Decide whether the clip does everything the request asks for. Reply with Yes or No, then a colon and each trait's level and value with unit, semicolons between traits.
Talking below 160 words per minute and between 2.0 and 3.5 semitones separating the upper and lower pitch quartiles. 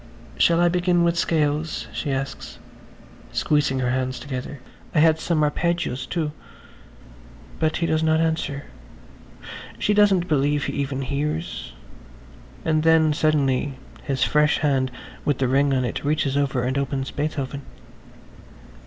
Yes: slow, 135 wpm; average, 3.0 semitones